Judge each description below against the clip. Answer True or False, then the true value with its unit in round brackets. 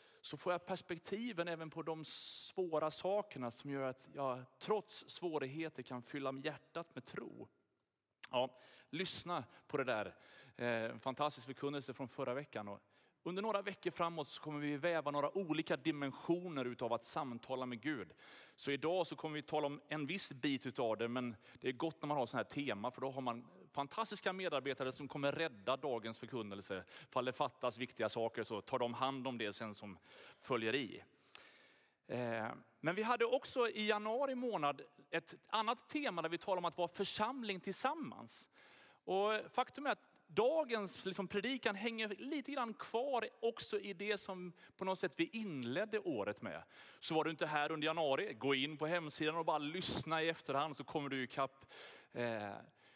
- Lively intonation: True (6.4 semitones)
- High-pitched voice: False (155 Hz)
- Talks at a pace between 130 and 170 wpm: False (180 wpm)